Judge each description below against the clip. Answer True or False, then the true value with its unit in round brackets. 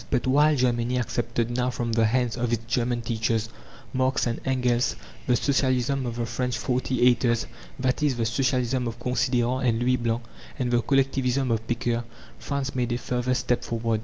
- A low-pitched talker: True (125 Hz)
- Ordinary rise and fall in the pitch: False (1.5 semitones)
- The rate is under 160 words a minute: False (180 wpm)